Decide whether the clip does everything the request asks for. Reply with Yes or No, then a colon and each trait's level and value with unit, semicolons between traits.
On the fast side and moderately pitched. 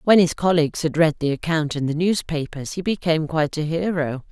Yes: fast, 210 wpm; medium, 160 Hz